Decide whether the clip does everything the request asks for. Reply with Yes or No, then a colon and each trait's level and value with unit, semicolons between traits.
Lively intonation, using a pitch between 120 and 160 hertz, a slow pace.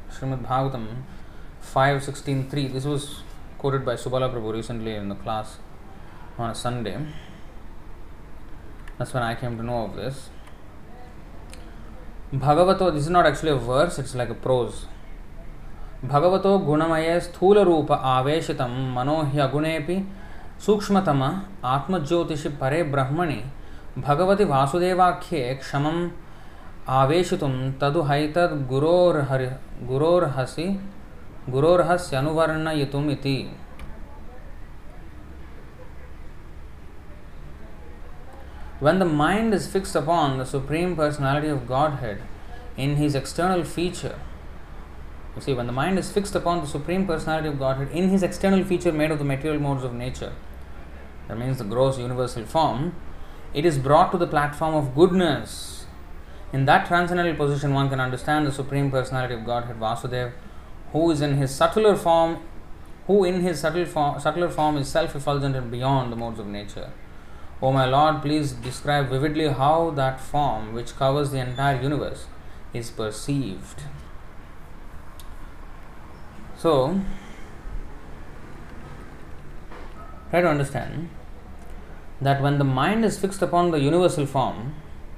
Yes: wide, 8.4 semitones; low, 135 Hz; slow, 95 wpm